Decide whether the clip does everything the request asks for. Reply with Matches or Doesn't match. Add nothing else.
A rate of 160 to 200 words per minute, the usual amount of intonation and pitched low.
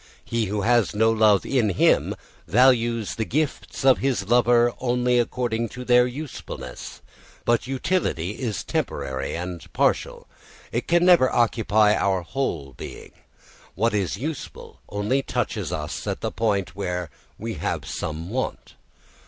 Doesn't match